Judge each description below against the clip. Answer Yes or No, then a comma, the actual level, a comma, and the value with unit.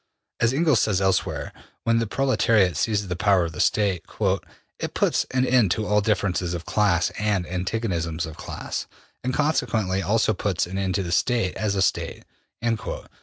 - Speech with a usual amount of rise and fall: Yes, average, 3.9 semitones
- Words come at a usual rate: Yes, average, 170 wpm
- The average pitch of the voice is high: No, low, 100 Hz